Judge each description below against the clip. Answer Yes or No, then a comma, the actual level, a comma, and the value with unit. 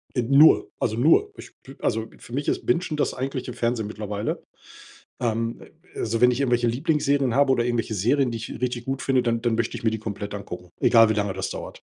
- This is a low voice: Yes, low, 120 Hz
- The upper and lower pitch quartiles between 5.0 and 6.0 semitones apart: No, average, 2.9 semitones